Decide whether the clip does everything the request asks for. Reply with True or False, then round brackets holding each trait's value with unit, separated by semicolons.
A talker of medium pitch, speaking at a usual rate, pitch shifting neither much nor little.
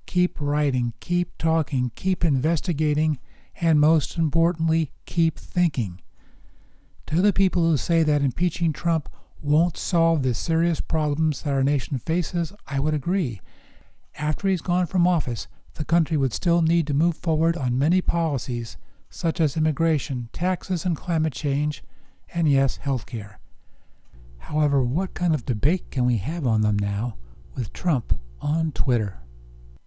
True (155 Hz; 145 wpm; 4.7 semitones)